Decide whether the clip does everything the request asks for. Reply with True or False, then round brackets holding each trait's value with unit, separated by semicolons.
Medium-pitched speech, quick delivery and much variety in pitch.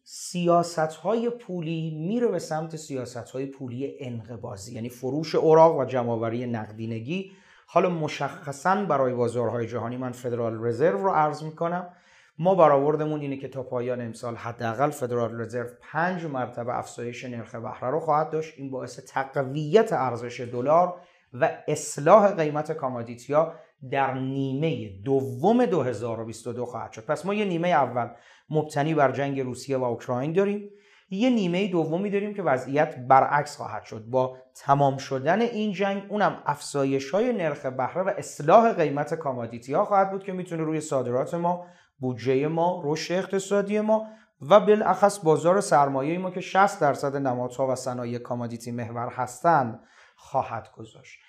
False (145 Hz; 145 wpm; 5.8 semitones)